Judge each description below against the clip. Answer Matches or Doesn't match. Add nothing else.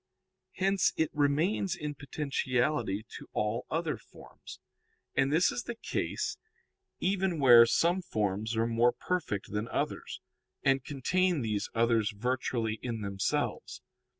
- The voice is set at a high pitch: Doesn't match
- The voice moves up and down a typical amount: Doesn't match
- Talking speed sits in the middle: Doesn't match